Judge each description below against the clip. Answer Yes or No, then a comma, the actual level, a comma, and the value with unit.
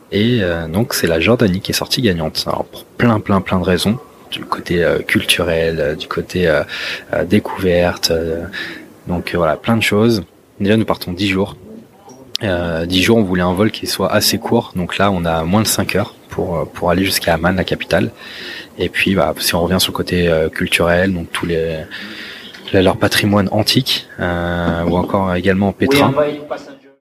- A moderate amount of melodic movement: Yes, average, 3.5 semitones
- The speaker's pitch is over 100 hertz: No, very low, 95 Hz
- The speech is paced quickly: No, average, 190 wpm